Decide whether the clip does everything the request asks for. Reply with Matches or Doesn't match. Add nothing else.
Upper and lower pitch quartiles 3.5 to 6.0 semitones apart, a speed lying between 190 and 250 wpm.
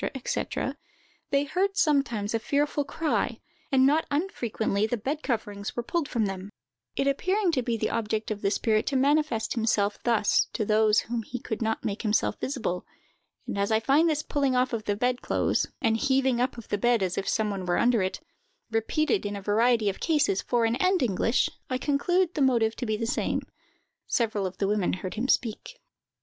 Matches